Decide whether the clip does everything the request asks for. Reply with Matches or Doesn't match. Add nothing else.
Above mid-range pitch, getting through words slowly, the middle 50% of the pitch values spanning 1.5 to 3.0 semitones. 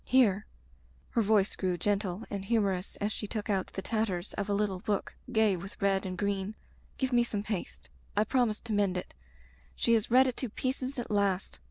Doesn't match